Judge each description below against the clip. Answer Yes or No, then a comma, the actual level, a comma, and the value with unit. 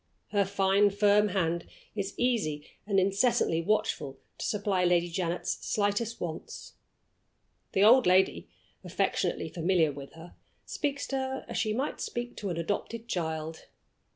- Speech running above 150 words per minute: No, average, 140 wpm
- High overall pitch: Yes, high, 195 Hz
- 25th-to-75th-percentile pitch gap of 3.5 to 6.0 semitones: Yes, average, 4.0 semitones